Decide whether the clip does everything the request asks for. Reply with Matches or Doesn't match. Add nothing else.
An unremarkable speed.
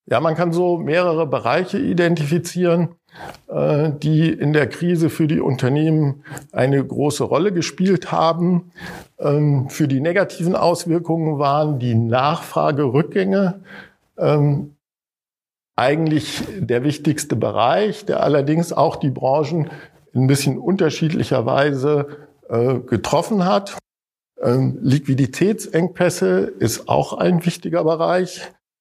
Doesn't match